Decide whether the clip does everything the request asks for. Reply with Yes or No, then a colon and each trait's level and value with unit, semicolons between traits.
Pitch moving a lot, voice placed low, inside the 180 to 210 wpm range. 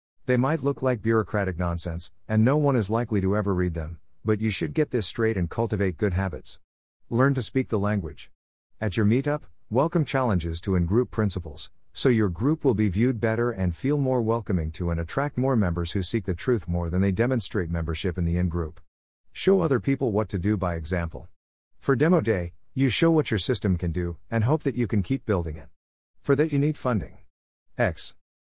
Yes: wide, 6.4 semitones; low, 105 Hz; fast, 205 wpm